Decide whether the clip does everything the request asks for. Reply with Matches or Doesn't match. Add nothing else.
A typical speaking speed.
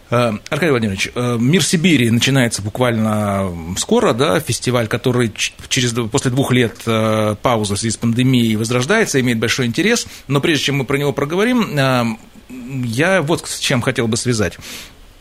Matches